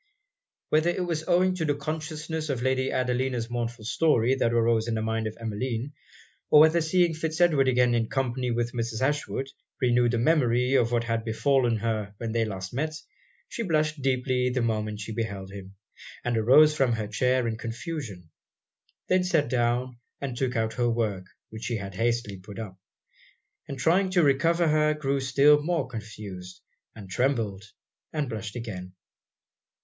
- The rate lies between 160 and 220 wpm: Yes, average, 170 wpm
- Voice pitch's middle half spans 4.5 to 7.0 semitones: Yes, average, 4.8 semitones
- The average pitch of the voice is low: Yes, low, 125 Hz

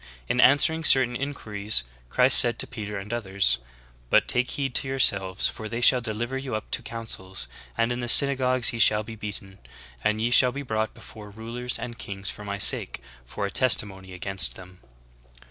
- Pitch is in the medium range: No, low, 110 Hz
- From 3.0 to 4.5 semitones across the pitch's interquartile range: Yes, average, 3.7 semitones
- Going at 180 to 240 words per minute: Yes, average, 185 wpm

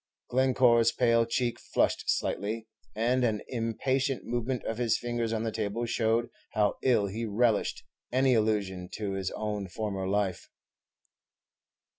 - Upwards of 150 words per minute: No, slow, 135 wpm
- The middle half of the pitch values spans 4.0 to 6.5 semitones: No, narrow, 2.4 semitones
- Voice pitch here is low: Yes, low, 115 Hz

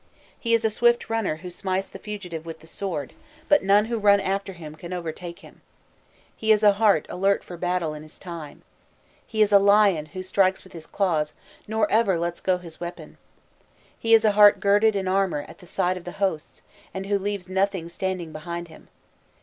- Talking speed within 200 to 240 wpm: Yes, fast, 205 wpm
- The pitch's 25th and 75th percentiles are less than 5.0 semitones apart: Yes, average, 3.2 semitones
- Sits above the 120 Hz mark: Yes, high, 190 Hz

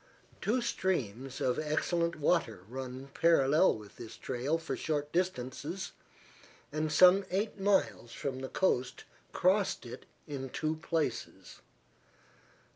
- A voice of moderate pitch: Yes, medium, 150 Hz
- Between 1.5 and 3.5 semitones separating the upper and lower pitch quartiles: No, average, 5.2 semitones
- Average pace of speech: No, slow, 120 wpm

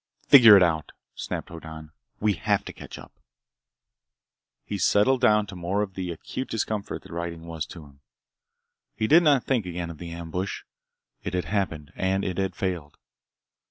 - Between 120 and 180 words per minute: Yes, average, 170 wpm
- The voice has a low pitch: Yes, very low, 90 Hz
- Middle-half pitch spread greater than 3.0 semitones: Yes, average, 3.8 semitones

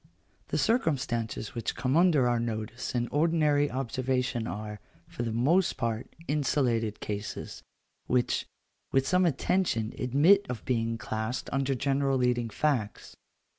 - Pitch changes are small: No, average, 3.9 semitones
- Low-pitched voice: Yes, low, 125 Hz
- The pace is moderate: No, slow, 130 wpm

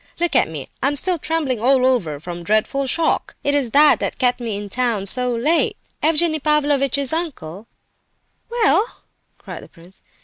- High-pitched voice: Yes, very high, 260 Hz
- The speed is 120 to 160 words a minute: No, average, 170 wpm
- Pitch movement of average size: No, wide, 5.9 semitones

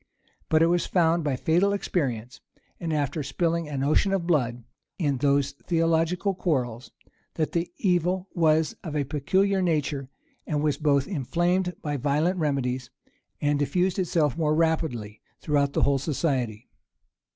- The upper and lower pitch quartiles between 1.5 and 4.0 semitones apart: Yes, average, 3.6 semitones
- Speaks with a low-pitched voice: No, medium, 155 Hz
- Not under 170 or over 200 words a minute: No, average, 145 wpm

